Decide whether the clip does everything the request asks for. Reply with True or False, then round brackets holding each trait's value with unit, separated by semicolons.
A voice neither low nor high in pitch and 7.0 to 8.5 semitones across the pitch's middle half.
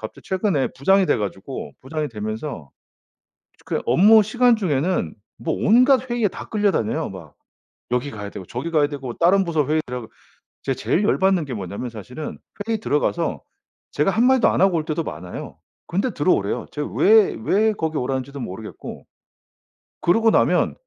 True (155 Hz; 8.1 semitones)